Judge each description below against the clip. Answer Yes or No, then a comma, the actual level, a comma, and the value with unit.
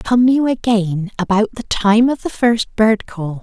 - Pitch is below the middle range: No, high, 220 Hz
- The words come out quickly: No, average, 195 wpm